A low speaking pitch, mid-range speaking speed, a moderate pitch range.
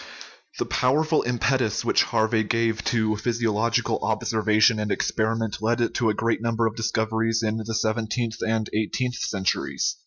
No: low, 115 Hz; average, 155 wpm; narrow, 1.2 semitones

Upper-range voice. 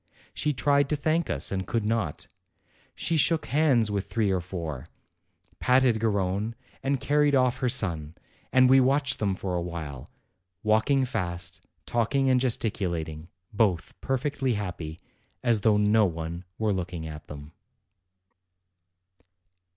No: low, 110 Hz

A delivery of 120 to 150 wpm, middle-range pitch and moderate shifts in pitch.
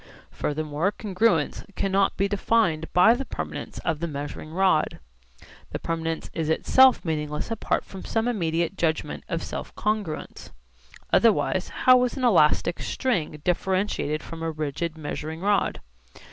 Yes: slow, 135 wpm; medium, 170 Hz; average, 4.7 semitones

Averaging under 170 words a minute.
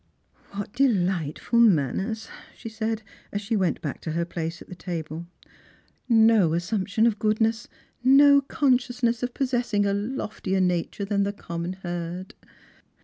Yes: average, 155 wpm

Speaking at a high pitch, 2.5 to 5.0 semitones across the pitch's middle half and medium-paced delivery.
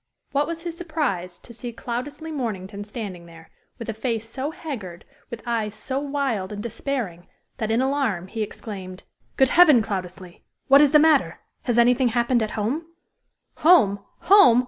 No: high, 235 Hz; wide, 5.5 semitones; average, 165 wpm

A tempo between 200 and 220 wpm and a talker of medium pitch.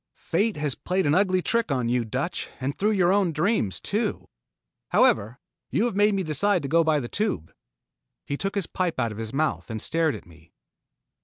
Yes: fast, 205 wpm; medium, 160 Hz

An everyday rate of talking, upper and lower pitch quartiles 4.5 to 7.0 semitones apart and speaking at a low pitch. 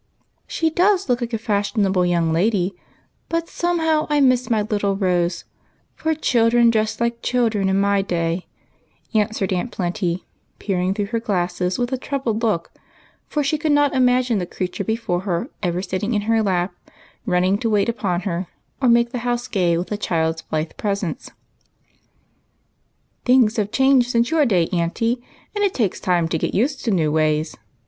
No: average, 180 wpm; average, 5.3 semitones; high, 210 Hz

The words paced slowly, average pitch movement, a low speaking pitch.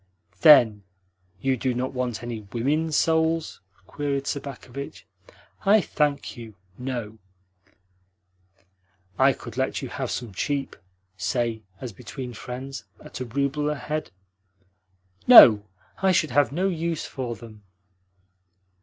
Yes: slow, 120 wpm; average, 3.7 semitones; low, 130 Hz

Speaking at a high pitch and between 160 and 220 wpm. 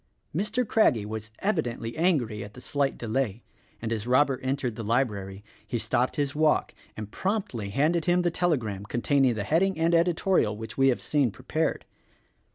No: low, 130 Hz; average, 165 wpm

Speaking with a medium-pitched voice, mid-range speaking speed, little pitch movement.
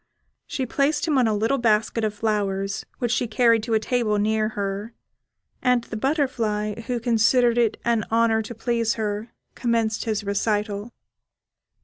No: high, 225 Hz; average, 155 wpm; narrow, 2.2 semitones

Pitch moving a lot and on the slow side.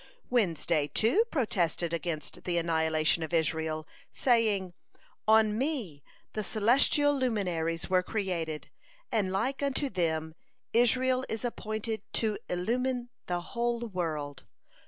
Yes: wide, 6.3 semitones; slow, 115 wpm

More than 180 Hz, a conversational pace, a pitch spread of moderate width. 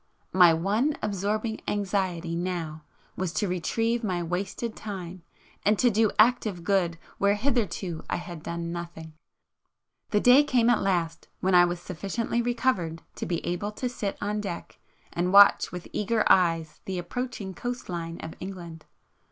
Yes: high, 190 Hz; average, 155 wpm; average, 3.9 semitones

